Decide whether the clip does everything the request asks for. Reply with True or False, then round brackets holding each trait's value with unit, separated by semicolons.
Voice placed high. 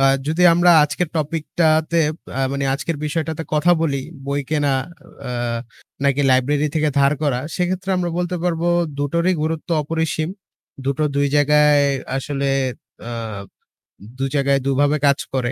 False (150 Hz)